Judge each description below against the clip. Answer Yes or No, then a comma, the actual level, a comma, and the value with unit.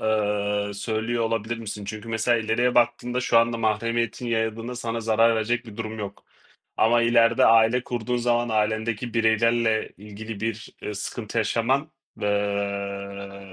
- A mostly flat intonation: Yes, narrow, 1.9 semitones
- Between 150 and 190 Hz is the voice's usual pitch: No, low, 110 Hz